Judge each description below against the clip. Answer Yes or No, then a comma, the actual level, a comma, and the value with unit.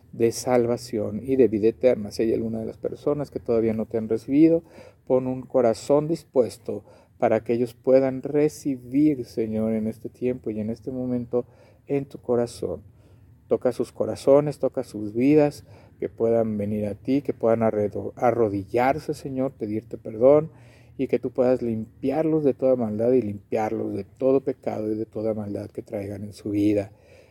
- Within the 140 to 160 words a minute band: No, average, 170 wpm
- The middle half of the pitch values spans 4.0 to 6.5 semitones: No, average, 3.3 semitones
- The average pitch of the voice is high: No, low, 120 Hz